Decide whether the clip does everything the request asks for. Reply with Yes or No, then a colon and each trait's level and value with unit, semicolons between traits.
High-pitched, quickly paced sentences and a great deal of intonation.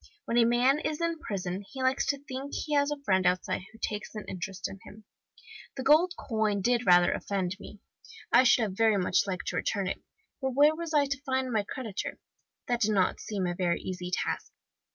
Yes: high, 225 Hz; fast, 215 wpm; wide, 5.7 semitones